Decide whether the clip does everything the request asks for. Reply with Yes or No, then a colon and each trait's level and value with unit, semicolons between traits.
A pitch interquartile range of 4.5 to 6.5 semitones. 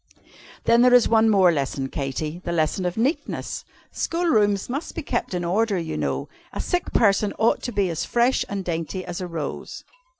Yes: wide, 5.4 semitones